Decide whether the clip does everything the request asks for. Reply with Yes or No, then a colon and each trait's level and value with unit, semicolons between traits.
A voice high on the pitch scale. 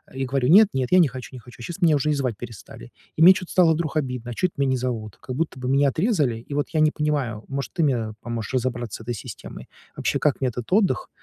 No: low, 135 Hz